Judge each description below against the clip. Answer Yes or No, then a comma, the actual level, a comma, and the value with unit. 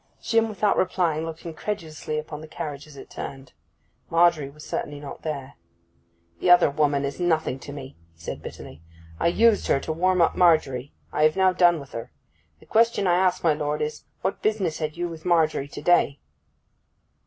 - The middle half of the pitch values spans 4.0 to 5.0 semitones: No, average, 3.3 semitones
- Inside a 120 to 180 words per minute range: No, average, 190 wpm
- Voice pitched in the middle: Yes, medium, 160 Hz